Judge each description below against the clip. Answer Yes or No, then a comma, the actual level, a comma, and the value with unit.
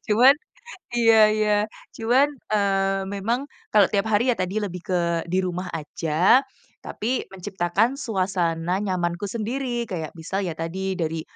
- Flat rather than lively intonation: No, average, 3.8 semitones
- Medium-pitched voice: No, high, 195 Hz